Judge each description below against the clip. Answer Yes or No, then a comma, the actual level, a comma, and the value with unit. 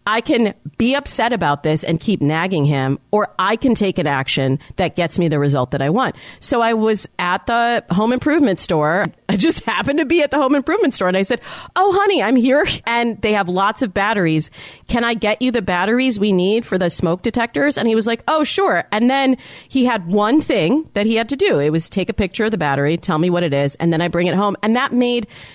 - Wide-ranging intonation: Yes, wide, 6.2 semitones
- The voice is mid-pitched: No, high, 215 Hz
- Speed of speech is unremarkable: No, fast, 250 wpm